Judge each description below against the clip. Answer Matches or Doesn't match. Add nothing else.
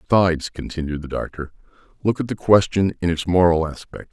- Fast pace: Doesn't match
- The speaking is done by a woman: Doesn't match